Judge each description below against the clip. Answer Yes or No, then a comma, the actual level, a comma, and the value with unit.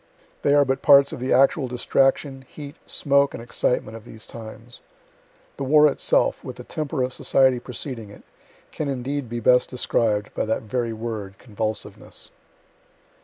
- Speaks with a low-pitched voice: Yes, low, 125 Hz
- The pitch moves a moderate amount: Yes, average, 3.5 semitones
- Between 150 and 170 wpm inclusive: Yes, average, 160 wpm